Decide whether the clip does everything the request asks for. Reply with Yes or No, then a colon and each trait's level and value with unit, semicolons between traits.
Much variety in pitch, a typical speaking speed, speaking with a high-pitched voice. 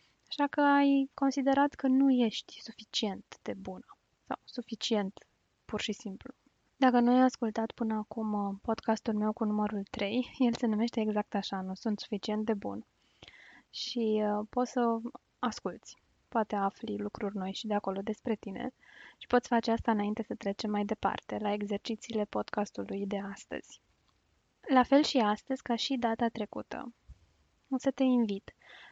No: average, 3.0 semitones; average, 155 wpm; high, 225 Hz